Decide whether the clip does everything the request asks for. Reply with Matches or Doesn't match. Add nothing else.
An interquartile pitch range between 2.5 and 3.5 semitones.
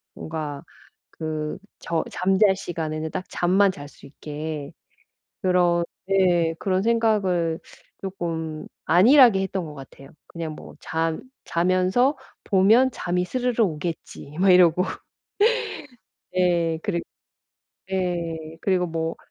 Matches